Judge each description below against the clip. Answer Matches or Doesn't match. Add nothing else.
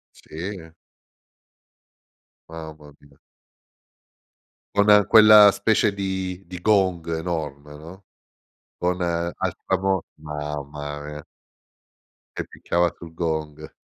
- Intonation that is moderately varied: Matches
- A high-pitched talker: Doesn't match